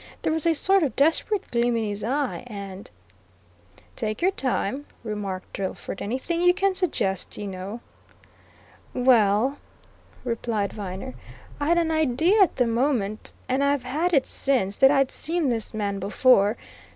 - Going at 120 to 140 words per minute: No, average, 155 wpm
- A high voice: Yes, high, 245 Hz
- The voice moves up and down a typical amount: No, wide, 6.5 semitones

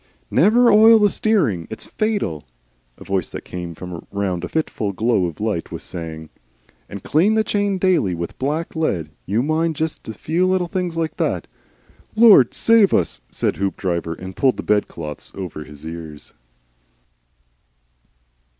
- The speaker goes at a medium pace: Yes, average, 160 wpm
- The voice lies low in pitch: Yes, low, 110 Hz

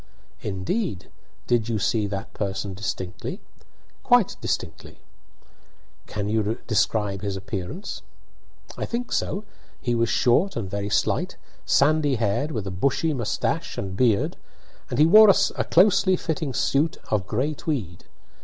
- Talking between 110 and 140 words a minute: Yes, slow, 135 wpm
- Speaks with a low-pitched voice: Yes, low, 115 Hz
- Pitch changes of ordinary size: No, wide, 7.4 semitones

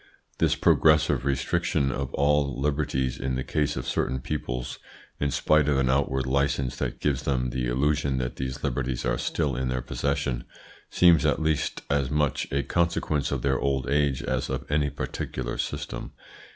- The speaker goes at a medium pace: Yes, average, 170 wpm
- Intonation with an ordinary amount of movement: No, narrow, 2.2 semitones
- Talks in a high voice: No, very low, 70 Hz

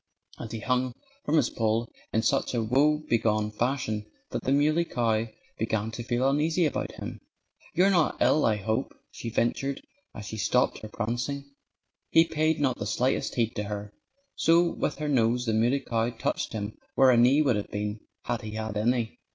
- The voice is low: Yes, low, 120 Hz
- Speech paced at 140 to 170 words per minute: No, average, 185 wpm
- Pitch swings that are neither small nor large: Yes, average, 4.1 semitones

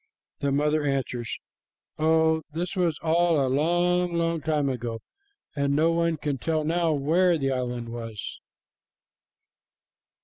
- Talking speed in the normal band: No, slow, 130 wpm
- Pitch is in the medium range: Yes, medium, 155 Hz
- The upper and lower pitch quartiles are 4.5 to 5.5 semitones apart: No, average, 3.5 semitones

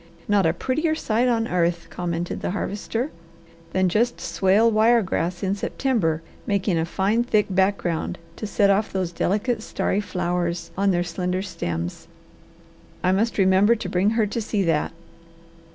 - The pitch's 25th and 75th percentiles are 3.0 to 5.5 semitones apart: Yes, average, 3.7 semitones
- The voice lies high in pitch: Yes, high, 195 Hz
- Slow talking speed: No, average, 155 wpm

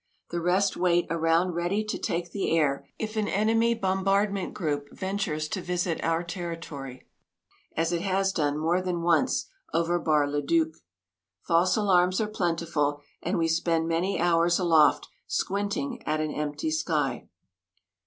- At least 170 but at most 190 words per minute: No, average, 150 wpm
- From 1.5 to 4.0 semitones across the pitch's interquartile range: Yes, average, 3.0 semitones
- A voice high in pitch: No, medium, 170 Hz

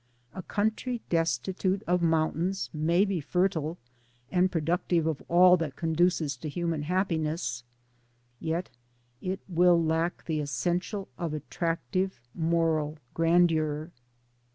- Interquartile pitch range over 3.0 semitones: No, narrow, 2.4 semitones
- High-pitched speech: No, medium, 170 Hz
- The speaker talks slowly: Yes, slow, 115 wpm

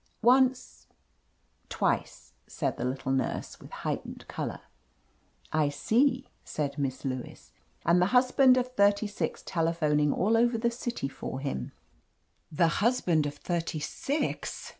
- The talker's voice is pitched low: No, medium, 170 Hz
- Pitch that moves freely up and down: Yes, wide, 8.8 semitones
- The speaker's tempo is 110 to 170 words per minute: Yes, average, 140 wpm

